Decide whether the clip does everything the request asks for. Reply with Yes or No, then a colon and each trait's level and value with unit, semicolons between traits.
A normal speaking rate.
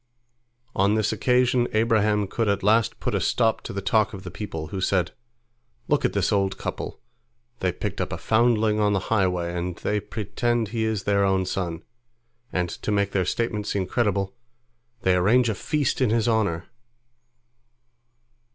Yes: average, 170 wpm